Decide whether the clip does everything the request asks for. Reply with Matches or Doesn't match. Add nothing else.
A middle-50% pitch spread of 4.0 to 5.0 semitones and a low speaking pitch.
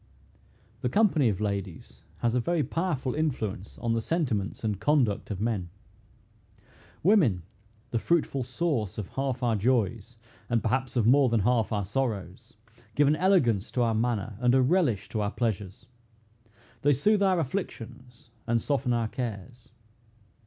Matches